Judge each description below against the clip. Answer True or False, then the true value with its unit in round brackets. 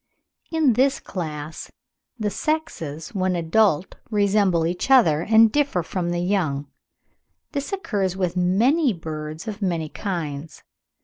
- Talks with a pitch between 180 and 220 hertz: True (185 Hz)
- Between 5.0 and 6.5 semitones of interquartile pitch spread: True (5.3 semitones)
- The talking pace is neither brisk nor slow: False (125 wpm)